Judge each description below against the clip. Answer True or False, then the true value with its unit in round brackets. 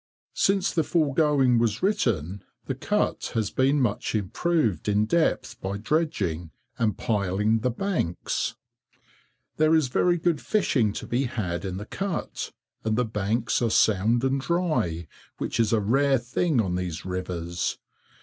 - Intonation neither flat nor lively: False (7.0 semitones)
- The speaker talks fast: False (150 wpm)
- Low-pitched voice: True (115 Hz)